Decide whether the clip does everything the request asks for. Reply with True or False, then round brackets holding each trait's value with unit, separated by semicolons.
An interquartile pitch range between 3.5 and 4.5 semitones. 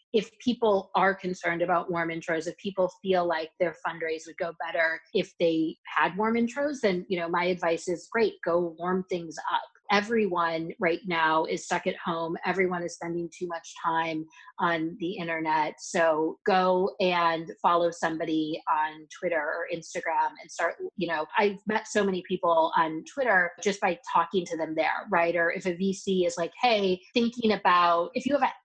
False (2.5 semitones)